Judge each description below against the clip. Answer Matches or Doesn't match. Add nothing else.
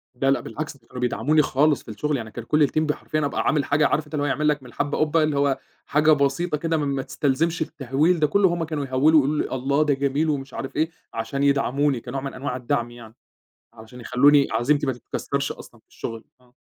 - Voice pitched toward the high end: Doesn't match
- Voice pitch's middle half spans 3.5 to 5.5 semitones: Doesn't match